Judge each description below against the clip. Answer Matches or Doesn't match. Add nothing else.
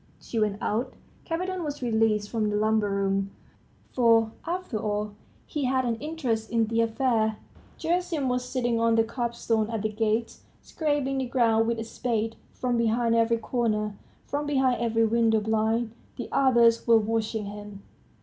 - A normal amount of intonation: Doesn't match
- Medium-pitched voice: Doesn't match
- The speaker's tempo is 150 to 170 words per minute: Matches